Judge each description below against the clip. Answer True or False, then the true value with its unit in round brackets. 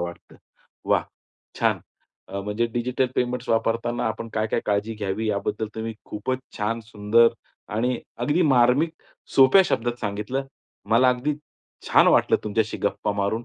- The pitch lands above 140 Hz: False (115 Hz)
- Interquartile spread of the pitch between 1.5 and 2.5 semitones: False (2.9 semitones)